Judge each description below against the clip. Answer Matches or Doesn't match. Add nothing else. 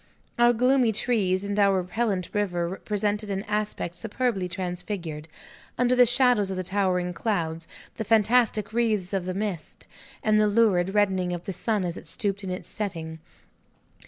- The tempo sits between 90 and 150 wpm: Doesn't match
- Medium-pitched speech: Doesn't match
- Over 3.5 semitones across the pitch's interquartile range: Doesn't match